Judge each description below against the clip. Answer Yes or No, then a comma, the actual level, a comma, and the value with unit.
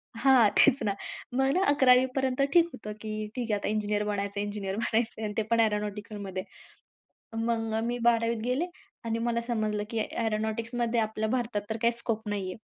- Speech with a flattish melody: Yes, narrow, 2.2 semitones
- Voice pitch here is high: Yes, high, 225 Hz